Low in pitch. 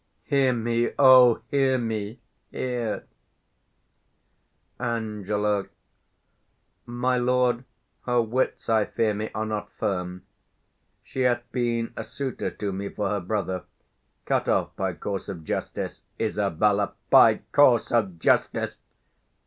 Yes: low, 115 Hz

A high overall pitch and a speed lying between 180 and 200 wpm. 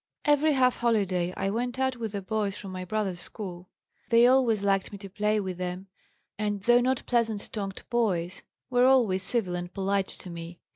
Yes: high, 205 Hz; average, 190 wpm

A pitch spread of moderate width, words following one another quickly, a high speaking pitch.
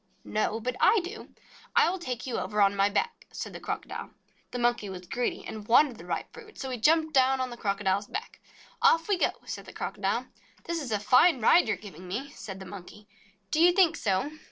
No: wide, 8.1 semitones; fast, 225 wpm; high, 245 Hz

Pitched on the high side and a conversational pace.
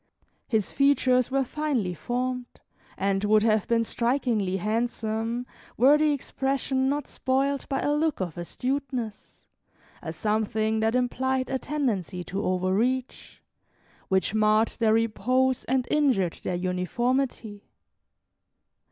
No: high, 240 Hz; slow, 115 wpm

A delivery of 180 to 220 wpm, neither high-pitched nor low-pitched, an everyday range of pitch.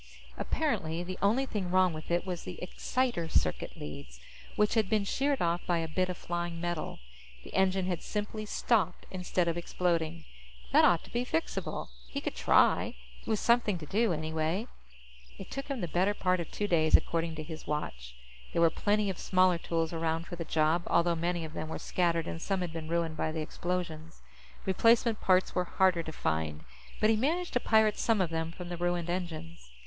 Yes: average, 200 wpm; medium, 175 Hz; average, 3.1 semitones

